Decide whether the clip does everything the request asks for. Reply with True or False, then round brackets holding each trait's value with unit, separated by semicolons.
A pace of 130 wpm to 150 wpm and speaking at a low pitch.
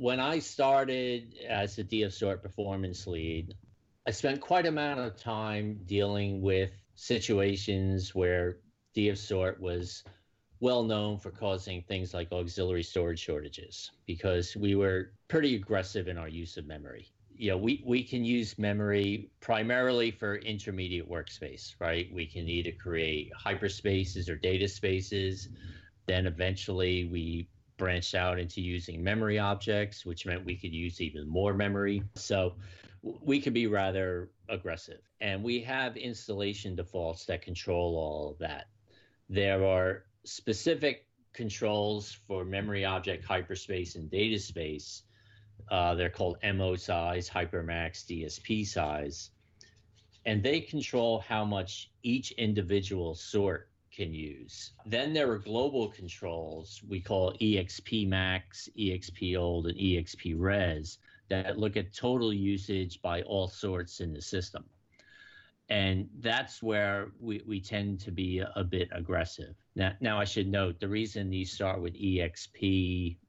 True (140 wpm; 95 Hz)